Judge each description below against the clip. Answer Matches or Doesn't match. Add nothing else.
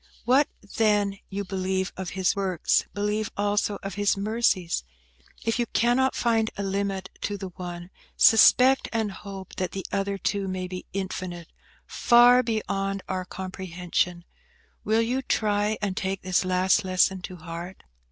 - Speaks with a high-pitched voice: Matches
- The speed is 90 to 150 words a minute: Matches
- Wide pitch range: Doesn't match